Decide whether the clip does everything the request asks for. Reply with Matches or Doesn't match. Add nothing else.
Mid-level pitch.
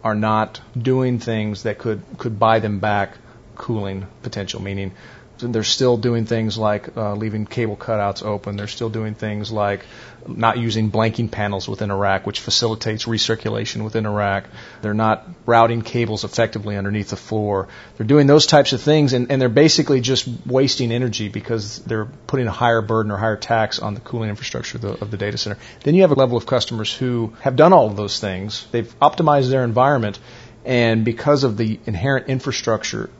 Doesn't match